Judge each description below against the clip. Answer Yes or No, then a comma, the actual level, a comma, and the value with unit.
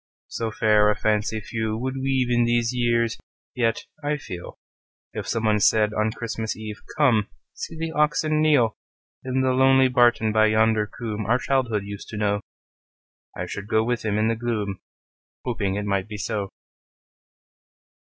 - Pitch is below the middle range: Yes, low, 110 Hz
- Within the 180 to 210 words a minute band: No, average, 150 wpm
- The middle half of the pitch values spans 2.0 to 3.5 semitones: Yes, average, 2.8 semitones